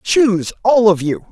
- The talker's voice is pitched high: Yes, high, 205 Hz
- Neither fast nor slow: Yes, average, 180 wpm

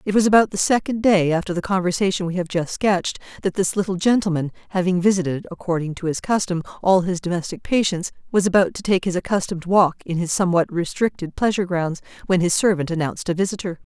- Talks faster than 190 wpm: Yes, average, 200 wpm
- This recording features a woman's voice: Yes, female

